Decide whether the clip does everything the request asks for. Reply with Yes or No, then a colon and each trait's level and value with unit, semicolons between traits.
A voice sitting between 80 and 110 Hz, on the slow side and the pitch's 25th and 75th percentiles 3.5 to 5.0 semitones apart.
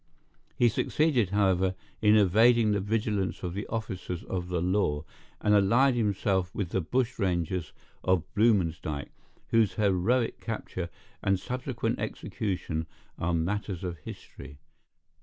Yes: low, 100 Hz; slow, 120 wpm; average, 3.9 semitones